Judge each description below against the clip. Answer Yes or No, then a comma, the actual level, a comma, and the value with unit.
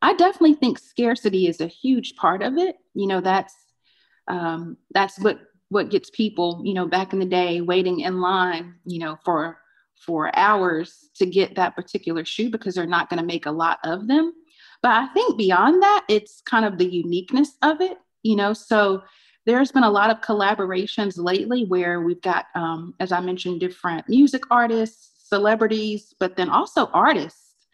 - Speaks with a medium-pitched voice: No, high, 200 Hz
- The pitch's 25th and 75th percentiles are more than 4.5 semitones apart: Yes, average, 5.3 semitones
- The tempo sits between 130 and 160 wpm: No, average, 185 wpm